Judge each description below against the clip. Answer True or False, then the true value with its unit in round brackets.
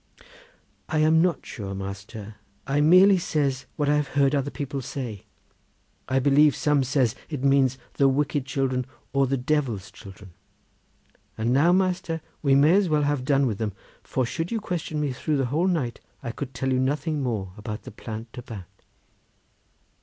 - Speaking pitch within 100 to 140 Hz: True (135 Hz)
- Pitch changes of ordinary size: True (3.7 semitones)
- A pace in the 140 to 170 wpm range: False (180 wpm)